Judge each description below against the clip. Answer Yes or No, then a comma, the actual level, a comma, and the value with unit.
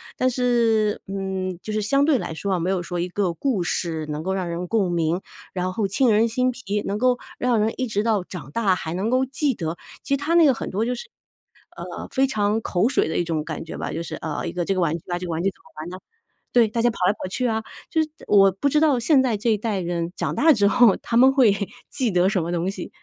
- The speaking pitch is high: Yes, high, 205 Hz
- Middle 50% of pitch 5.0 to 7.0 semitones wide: Yes, wide, 5.6 semitones